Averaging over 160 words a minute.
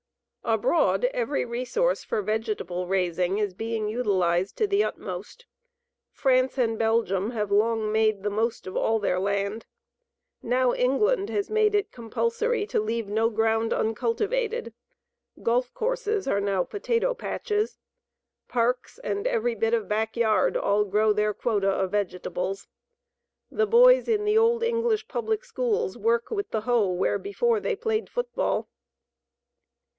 No: average, 140 wpm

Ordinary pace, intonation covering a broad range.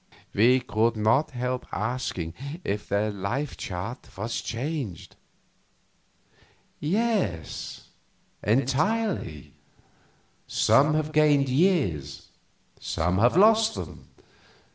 No: slow, 85 wpm; wide, 7.0 semitones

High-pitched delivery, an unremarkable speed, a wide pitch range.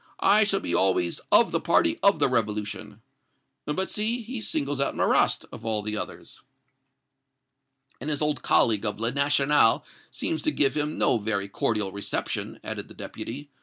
No: low, 125 Hz; average, 165 wpm; wide, 6.0 semitones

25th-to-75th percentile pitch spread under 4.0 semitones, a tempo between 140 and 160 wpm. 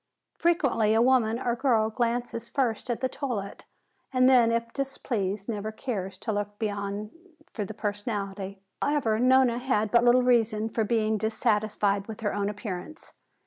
Yes: average, 2.9 semitones; average, 155 wpm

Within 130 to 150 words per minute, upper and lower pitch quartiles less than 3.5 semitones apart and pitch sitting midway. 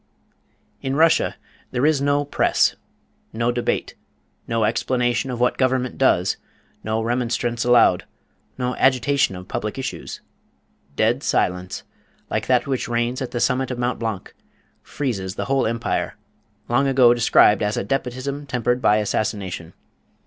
No: average, 140 wpm; average, 2.9 semitones; low, 120 Hz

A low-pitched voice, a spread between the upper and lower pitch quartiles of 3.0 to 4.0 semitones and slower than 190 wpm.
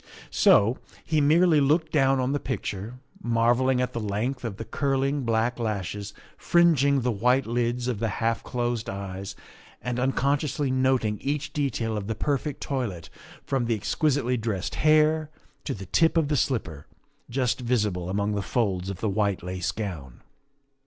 No: low, 120 Hz; average, 4.8 semitones; average, 165 wpm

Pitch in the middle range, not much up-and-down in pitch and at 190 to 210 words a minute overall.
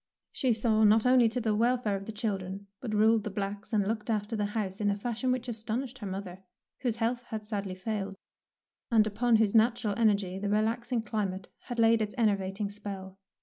No: high, 215 Hz; narrow, 2.3 semitones; average, 195 wpm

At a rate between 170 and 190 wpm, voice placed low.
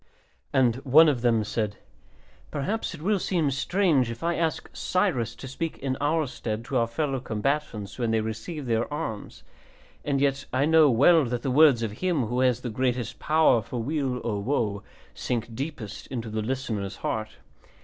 Yes: average, 180 wpm; low, 130 Hz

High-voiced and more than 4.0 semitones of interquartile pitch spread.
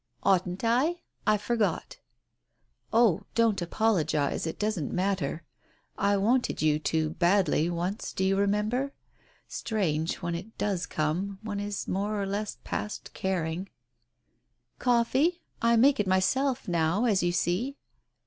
Yes: high, 200 Hz; average, 4.4 semitones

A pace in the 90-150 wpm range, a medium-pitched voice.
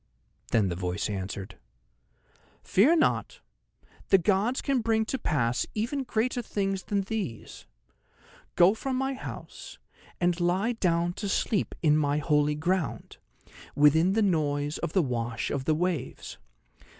Yes: average, 140 wpm; medium, 175 Hz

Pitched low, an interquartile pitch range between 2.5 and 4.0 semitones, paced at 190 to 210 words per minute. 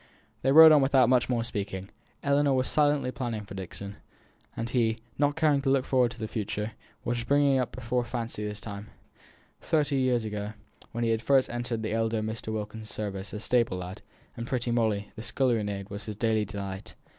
Yes: low, 115 Hz; average, 3.5 semitones; average, 200 wpm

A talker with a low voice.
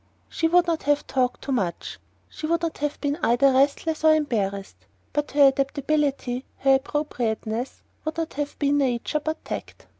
No: very high, 280 Hz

